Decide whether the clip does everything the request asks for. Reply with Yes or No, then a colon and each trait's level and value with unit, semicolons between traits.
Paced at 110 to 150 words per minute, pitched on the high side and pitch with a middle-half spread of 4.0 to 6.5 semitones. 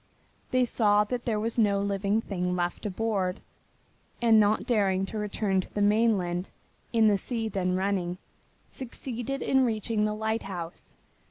No: average, 145 wpm; high, 210 Hz; average, 2.8 semitones